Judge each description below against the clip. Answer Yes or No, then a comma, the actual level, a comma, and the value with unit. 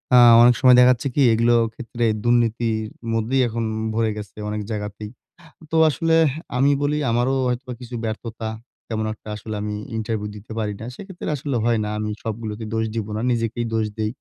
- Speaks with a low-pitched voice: Yes, low, 115 Hz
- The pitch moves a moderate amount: No, narrow, 2.2 semitones